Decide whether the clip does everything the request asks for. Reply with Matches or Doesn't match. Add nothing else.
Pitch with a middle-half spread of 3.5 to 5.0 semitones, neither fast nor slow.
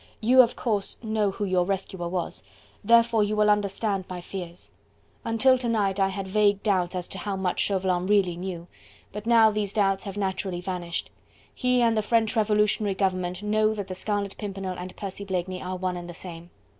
Doesn't match